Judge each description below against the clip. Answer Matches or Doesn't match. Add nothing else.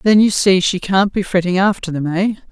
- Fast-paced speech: Matches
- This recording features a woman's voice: Matches